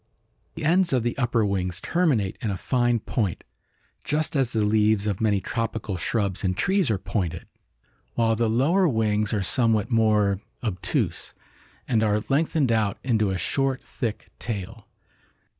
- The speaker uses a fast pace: No, average, 155 wpm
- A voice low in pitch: Yes, low, 110 Hz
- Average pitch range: Yes, average, 3.6 semitones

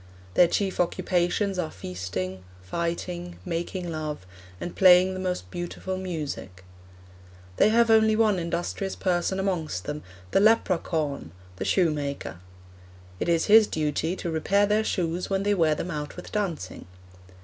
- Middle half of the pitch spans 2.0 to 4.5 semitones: Yes, average, 3.8 semitones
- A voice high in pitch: No, medium, 175 Hz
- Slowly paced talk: No, average, 145 wpm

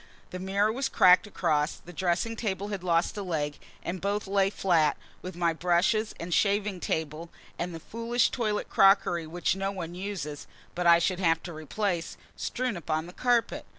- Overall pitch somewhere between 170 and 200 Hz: Yes, medium, 185 Hz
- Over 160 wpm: Yes, average, 180 wpm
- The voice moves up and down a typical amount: Yes, average, 3.2 semitones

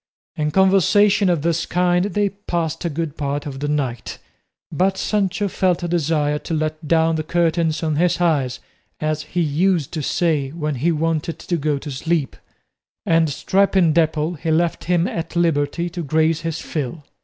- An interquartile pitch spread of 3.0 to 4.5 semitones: No, narrow, 2.5 semitones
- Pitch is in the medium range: Yes, medium, 165 Hz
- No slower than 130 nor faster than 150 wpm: No, average, 175 wpm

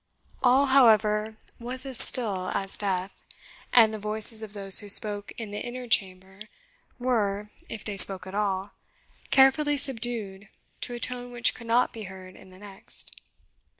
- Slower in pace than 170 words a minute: Yes, average, 160 wpm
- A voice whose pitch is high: Yes, high, 215 Hz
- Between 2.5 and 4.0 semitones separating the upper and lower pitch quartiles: Yes, average, 3.6 semitones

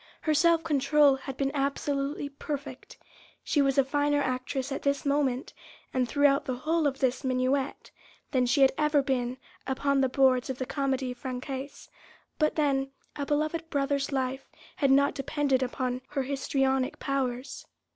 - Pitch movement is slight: Yes, narrow, 1.6 semitones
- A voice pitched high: Yes, very high, 275 Hz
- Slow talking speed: No, average, 155 wpm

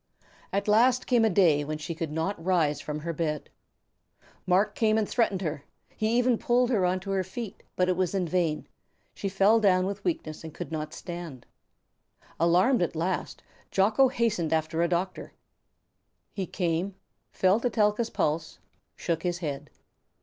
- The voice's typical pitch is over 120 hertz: Yes, medium, 185 Hz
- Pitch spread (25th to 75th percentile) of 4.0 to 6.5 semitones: Yes, average, 4.4 semitones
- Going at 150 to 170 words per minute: Yes, average, 165 wpm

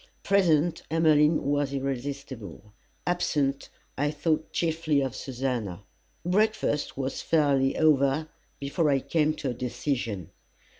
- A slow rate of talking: Yes, slow, 110 wpm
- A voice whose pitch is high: No, medium, 145 Hz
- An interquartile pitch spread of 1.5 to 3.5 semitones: Yes, average, 2.8 semitones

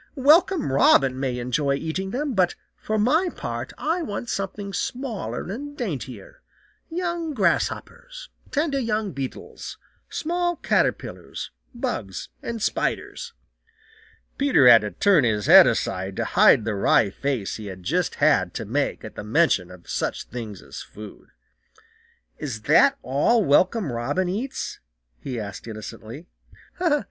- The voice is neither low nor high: Yes, medium, 175 Hz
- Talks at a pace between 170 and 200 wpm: No, slow, 135 wpm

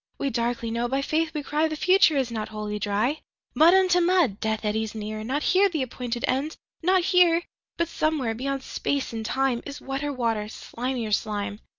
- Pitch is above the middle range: Yes, very high, 265 Hz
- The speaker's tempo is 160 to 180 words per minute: Yes, average, 170 wpm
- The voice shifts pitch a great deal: Yes, wide, 6.0 semitones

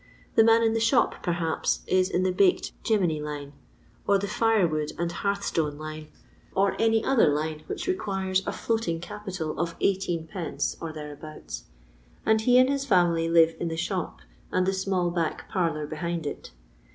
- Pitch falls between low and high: Yes, medium, 175 Hz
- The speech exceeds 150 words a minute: Yes, average, 180 wpm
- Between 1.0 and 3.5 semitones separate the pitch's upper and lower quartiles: No, average, 4.0 semitones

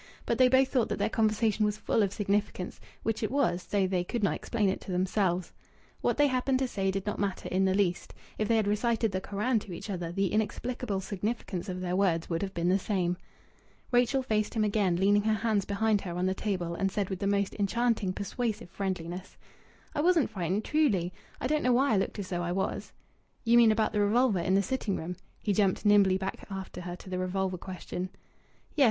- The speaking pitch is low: No, high, 200 Hz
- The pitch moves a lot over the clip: No, average, 3.0 semitones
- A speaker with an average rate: No, fast, 220 wpm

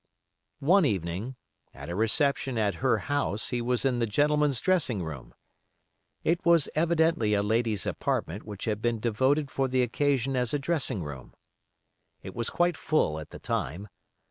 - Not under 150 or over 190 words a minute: Yes, average, 165 wpm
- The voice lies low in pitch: Yes, low, 125 Hz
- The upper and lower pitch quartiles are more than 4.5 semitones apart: Yes, wide, 5.6 semitones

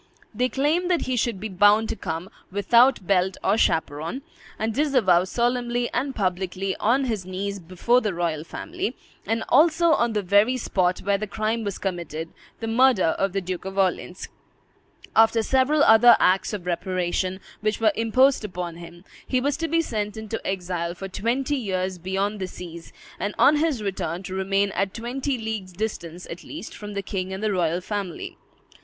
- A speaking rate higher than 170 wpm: Yes, average, 180 wpm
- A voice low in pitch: No, high, 205 Hz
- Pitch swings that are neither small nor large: Yes, average, 4.5 semitones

